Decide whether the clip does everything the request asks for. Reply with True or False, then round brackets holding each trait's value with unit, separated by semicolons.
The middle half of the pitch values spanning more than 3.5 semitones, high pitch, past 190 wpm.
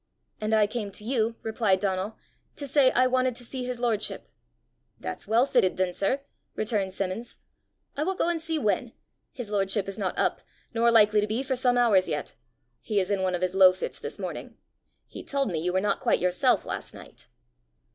True (4.4 semitones; 215 Hz; 205 wpm)